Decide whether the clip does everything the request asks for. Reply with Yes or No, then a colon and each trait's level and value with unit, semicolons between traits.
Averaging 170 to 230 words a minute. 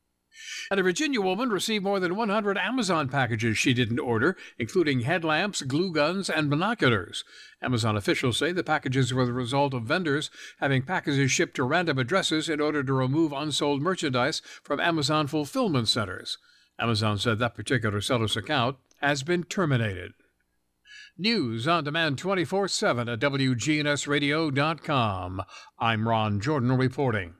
No: average, 140 wpm